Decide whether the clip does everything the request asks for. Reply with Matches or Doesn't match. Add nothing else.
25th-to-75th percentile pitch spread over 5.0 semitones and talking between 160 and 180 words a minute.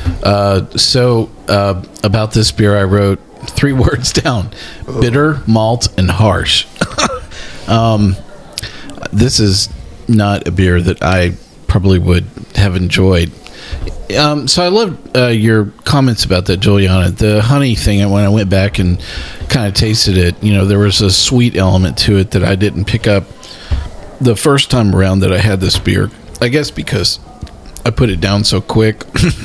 Doesn't match